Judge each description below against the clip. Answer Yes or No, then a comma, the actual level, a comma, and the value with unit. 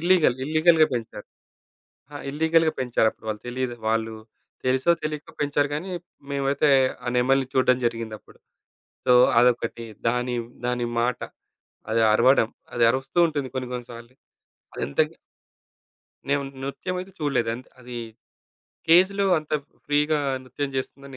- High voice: No, low, 130 Hz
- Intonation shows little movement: No, average, 3.6 semitones